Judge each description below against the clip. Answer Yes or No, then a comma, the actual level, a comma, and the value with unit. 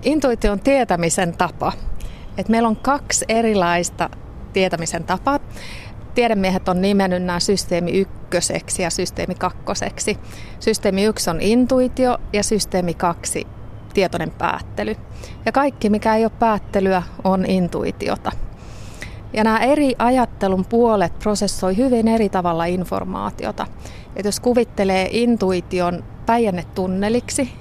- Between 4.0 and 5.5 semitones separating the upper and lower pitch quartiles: Yes, average, 4.4 semitones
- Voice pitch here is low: No, high, 190 Hz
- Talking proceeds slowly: No, average, 115 wpm